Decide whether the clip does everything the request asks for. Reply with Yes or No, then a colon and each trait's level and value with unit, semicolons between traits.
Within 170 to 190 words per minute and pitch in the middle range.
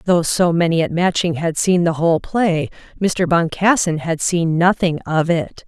Yes: average, 180 wpm; medium, 170 Hz